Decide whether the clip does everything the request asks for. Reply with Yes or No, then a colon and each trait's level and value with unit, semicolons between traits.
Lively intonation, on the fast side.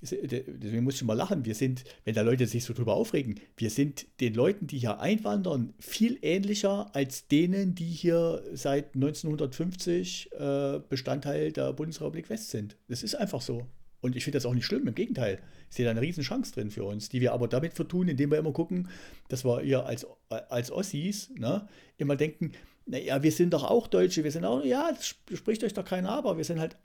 Yes: wide, 6.4 semitones; fast, 205 wpm